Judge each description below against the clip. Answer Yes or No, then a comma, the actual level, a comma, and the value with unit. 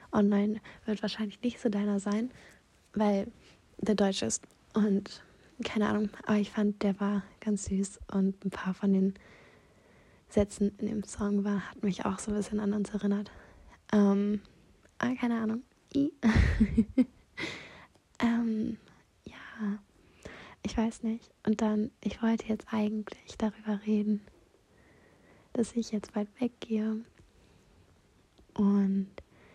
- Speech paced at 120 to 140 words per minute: Yes, average, 130 wpm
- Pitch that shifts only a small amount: Yes, narrow, 1.6 semitones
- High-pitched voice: Yes, high, 210 Hz